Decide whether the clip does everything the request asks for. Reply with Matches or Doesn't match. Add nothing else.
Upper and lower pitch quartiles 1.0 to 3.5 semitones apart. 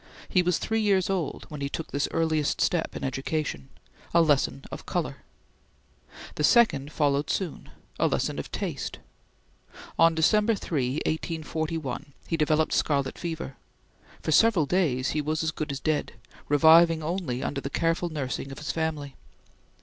Matches